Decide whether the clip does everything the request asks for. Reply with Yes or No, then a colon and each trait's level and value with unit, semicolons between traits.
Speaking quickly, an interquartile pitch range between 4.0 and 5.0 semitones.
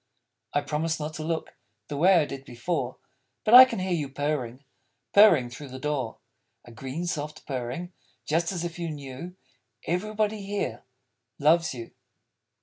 No: average, 160 wpm; average, 4.7 semitones